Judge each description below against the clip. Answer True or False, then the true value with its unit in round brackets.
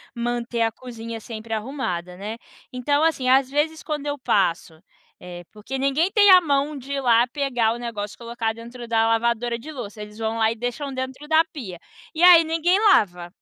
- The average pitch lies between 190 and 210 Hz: False (240 Hz)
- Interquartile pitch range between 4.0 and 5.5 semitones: True (4.4 semitones)